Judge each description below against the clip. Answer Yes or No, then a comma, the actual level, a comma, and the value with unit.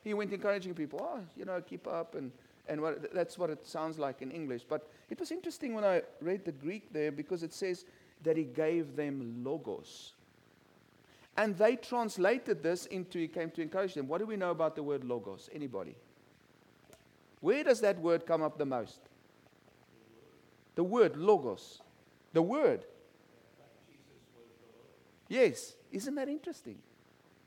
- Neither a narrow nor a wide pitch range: No, wide, 5.9 semitones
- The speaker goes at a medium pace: Yes, average, 160 wpm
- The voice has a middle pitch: Yes, medium, 175 Hz